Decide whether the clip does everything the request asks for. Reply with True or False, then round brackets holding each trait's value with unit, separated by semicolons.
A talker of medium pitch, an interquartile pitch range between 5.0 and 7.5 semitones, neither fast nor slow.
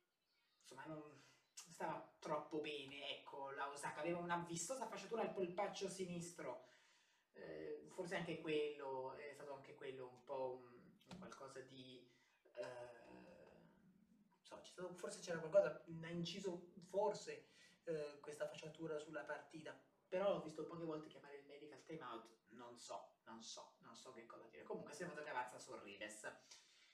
True (155 Hz; 5.3 semitones; 150 wpm)